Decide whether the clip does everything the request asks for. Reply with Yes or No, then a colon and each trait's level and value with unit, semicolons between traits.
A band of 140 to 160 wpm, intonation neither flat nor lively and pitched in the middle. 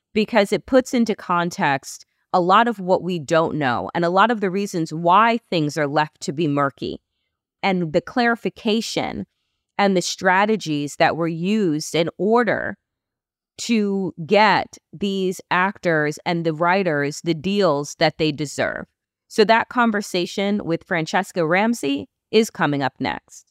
Yes: average, 150 wpm; average, 4.3 semitones; medium, 180 Hz